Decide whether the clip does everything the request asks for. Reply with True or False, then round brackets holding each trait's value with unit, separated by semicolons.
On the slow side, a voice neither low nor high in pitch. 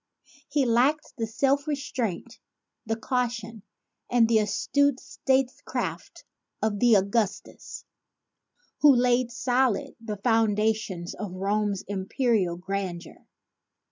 False (105 wpm; 225 Hz)